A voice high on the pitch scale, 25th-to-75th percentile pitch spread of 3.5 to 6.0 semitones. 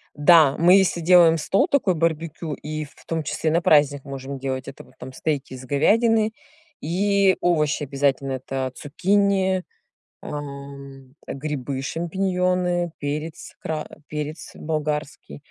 No: medium, 155 Hz; average, 4.1 semitones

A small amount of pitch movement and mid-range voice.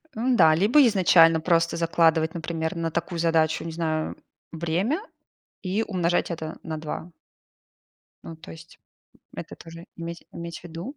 Yes: narrow, 1.5 semitones; medium, 165 Hz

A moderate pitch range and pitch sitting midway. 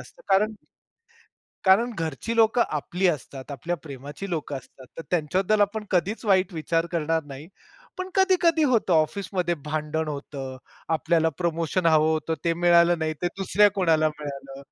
Yes: average, 4.1 semitones; medium, 170 Hz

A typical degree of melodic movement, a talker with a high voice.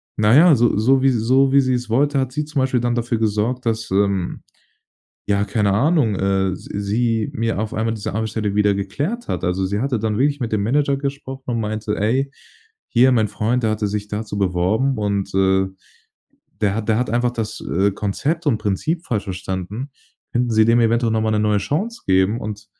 No: average, 3.8 semitones; low, 110 Hz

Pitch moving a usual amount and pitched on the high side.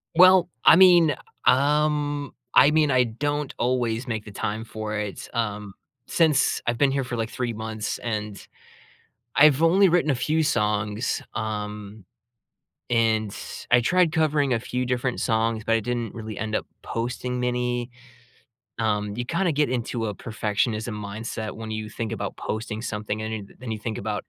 No: average, 4.2 semitones; low, 115 Hz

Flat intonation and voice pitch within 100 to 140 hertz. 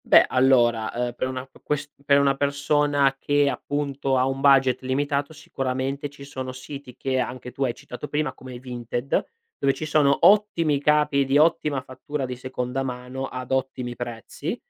Yes: narrow, 2.0 semitones; low, 135 Hz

